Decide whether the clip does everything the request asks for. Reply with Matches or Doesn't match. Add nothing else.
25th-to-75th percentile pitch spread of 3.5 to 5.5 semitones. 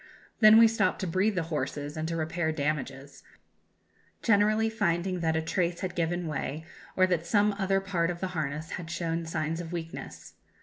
Doesn't match